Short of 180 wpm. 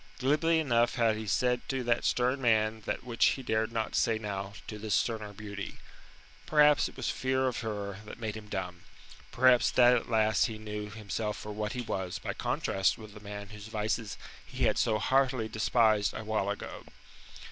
No: average, 190 wpm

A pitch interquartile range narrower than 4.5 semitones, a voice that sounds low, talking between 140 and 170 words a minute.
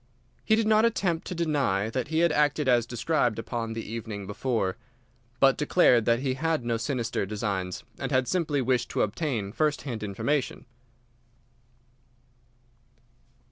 No: average, 5.2 semitones; low, 125 Hz; average, 145 wpm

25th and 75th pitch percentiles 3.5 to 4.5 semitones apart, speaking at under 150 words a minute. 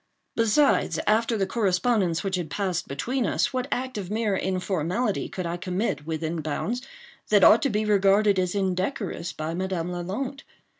No: average, 4.0 semitones; average, 160 wpm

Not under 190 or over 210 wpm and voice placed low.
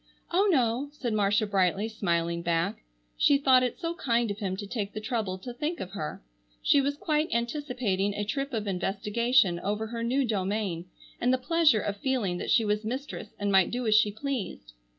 No: average, 195 wpm; high, 220 Hz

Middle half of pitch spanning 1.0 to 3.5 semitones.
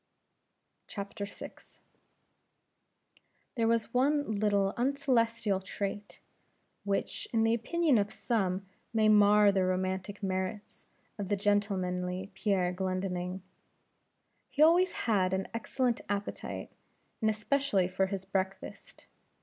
Yes: average, 3.1 semitones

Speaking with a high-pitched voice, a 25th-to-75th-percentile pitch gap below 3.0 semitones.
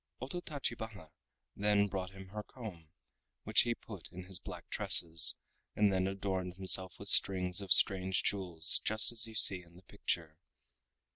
No: very low, 95 Hz; narrow, 2.5 semitones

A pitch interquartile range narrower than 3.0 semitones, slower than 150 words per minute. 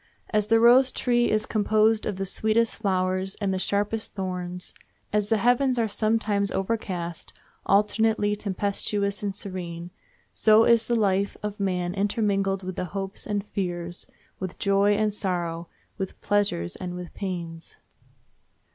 Yes: narrow, 2.6 semitones; average, 140 wpm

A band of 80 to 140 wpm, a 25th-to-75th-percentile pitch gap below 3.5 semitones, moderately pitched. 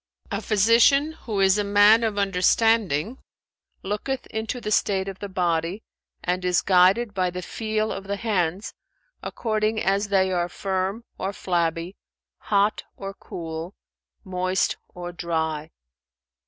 No: slow, 135 wpm; average, 3.1 semitones; high, 195 Hz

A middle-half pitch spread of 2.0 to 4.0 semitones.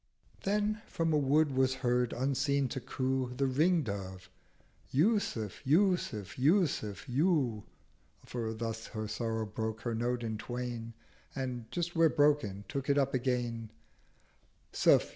No: average, 4.5 semitones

